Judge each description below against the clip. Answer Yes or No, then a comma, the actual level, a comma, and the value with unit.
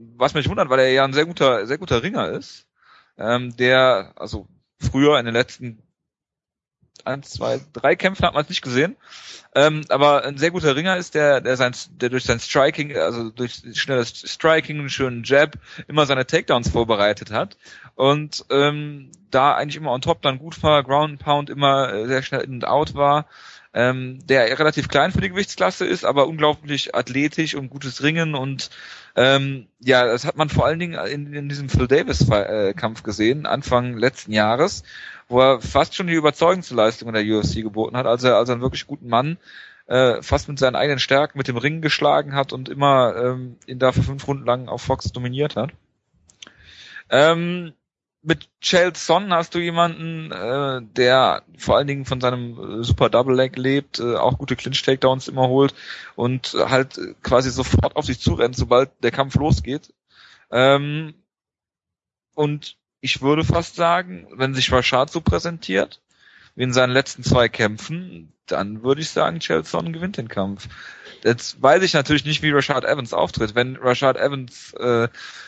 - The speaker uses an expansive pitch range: No, average, 3.3 semitones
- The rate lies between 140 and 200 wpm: Yes, average, 180 wpm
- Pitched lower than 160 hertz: Yes, low, 135 Hz